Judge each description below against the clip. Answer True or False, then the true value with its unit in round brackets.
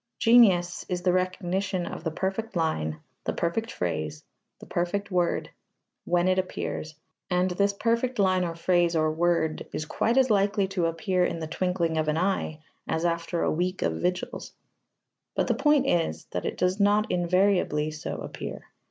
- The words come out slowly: False (170 wpm)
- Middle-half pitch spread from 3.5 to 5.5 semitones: False (3.1 semitones)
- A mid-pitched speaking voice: True (180 Hz)